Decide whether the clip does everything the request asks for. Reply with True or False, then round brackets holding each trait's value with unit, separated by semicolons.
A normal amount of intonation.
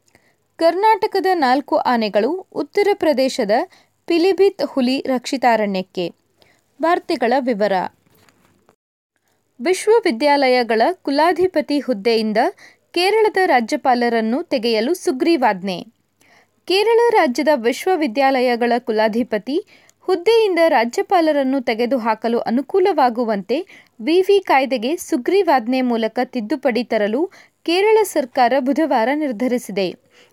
False (6.6 semitones)